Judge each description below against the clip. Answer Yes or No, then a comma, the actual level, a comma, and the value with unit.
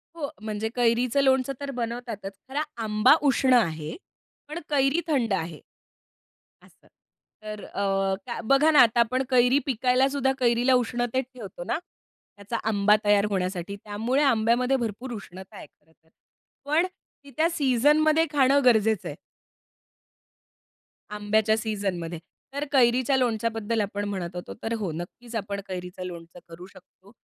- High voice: Yes, high, 230 Hz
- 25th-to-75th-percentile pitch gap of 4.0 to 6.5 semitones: Yes, average, 4.6 semitones